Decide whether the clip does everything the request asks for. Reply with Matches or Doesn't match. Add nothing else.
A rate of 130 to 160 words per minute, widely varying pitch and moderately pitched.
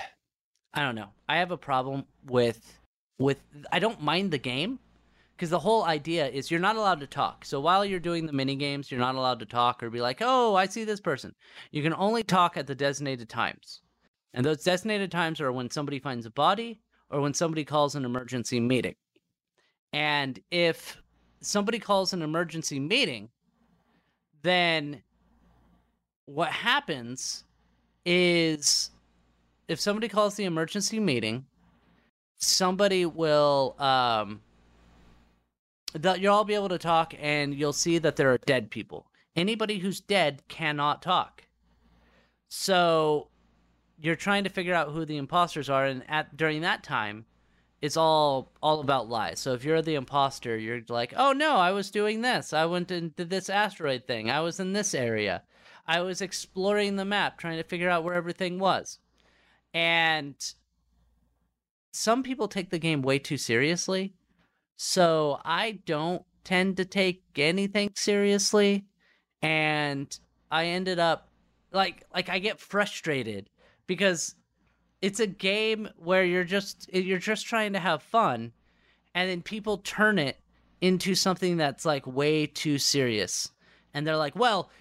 Matches